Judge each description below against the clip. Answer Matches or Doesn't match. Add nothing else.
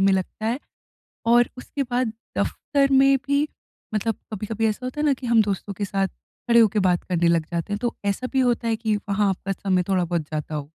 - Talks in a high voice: Matches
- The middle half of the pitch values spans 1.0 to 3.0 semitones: Doesn't match